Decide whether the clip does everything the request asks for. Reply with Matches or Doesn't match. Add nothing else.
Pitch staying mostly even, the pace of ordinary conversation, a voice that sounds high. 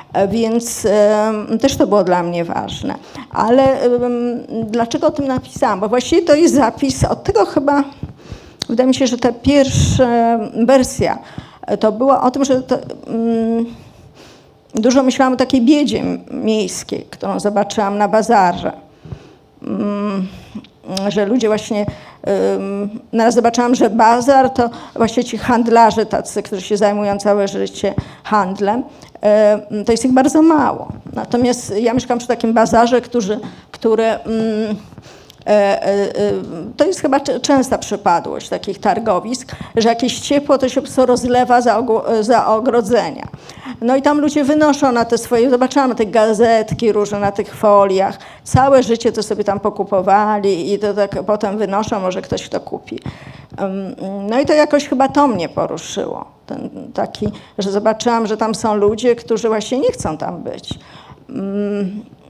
Doesn't match